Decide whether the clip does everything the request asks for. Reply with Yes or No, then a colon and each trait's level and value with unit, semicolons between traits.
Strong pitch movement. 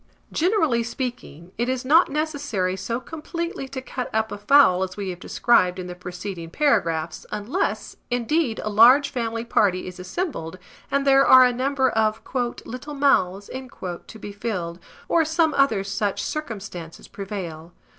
Yes: wide, 6.8 semitones